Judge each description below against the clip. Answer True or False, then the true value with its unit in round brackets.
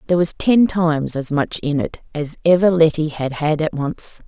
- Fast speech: True (210 wpm)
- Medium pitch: True (160 Hz)